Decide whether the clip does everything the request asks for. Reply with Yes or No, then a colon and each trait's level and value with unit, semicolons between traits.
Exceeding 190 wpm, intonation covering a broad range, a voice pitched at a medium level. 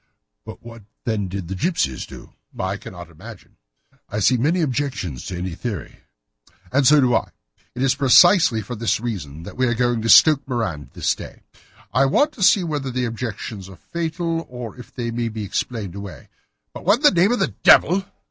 No: average, 200 wpm; wide, 6.3 semitones; low, 120 Hz